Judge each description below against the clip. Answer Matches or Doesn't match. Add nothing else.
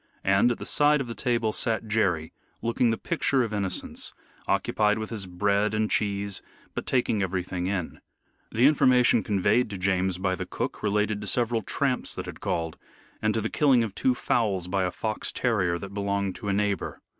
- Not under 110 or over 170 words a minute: Doesn't match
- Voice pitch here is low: Matches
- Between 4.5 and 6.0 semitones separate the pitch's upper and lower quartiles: Doesn't match